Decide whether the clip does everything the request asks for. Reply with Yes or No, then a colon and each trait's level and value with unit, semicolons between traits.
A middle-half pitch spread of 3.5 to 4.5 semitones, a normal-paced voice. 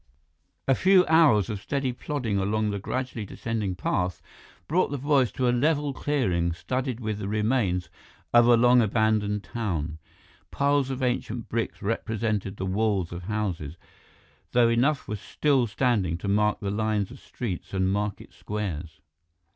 Yes: average, 4.2 semitones; average, 155 wpm